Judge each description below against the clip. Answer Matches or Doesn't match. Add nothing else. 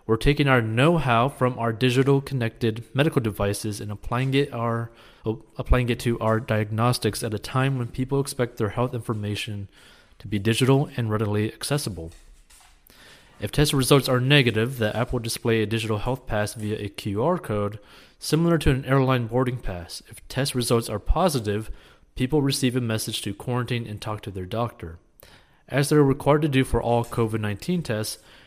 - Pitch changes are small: Doesn't match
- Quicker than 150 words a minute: Matches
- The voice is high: Doesn't match